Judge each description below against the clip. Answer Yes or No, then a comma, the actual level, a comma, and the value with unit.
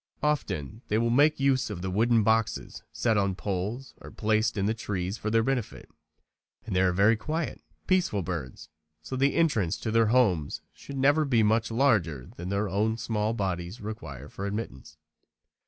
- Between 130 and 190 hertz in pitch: No, low, 110 Hz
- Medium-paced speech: Yes, average, 170 wpm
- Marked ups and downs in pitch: No, average, 4.1 semitones